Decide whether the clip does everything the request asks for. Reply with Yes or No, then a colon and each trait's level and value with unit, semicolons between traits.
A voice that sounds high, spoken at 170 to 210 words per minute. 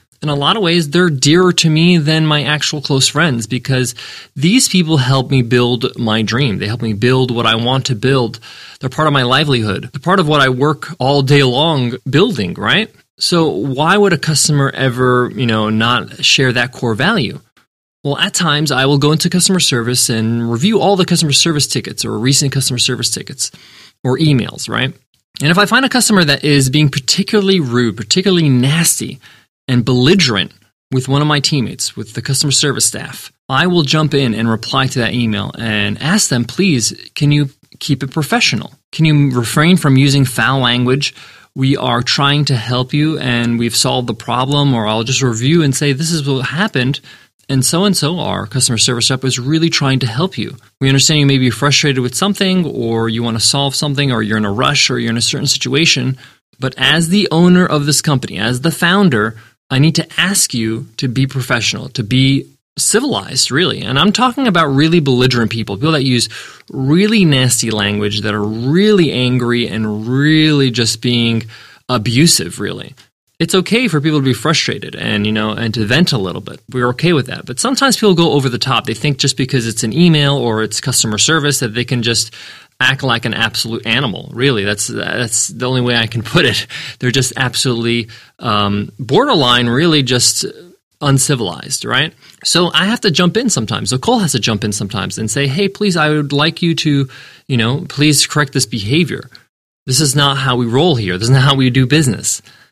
No: low, 135 Hz; fast, 205 wpm